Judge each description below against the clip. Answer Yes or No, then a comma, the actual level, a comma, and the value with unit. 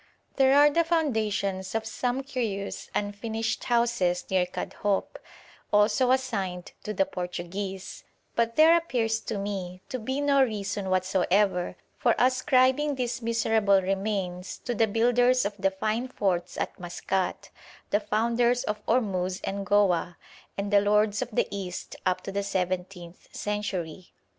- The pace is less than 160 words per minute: Yes, average, 140 wpm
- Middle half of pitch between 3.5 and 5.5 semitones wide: Yes, average, 4.0 semitones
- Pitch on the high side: Yes, high, 205 Hz